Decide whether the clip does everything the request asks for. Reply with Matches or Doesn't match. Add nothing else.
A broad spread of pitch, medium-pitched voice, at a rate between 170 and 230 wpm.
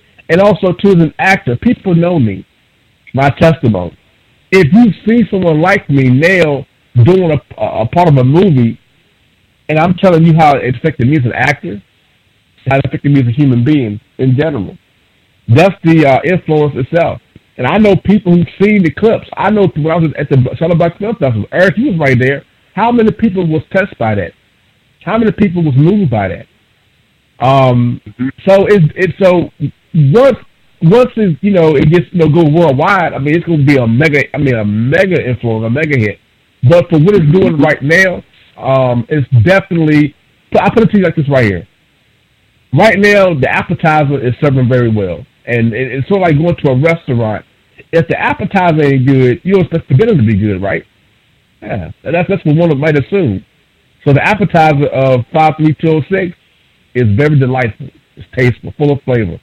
Matches